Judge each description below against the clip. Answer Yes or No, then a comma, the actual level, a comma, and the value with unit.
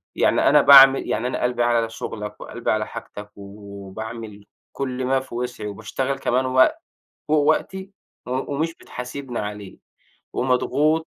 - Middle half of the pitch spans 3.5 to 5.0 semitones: Yes, average, 4.4 semitones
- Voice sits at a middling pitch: No, low, 125 Hz